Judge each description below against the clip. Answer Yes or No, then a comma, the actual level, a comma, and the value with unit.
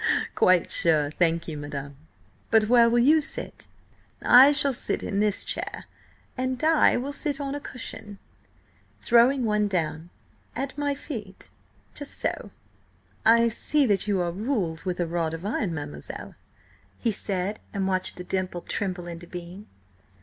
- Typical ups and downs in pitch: No, wide, 6.3 semitones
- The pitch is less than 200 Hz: No, high, 205 Hz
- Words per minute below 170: Yes, average, 145 wpm